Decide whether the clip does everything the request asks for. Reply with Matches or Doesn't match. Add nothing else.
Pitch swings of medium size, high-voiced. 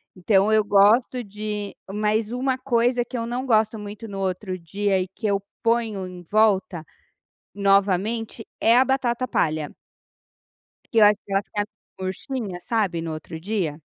Matches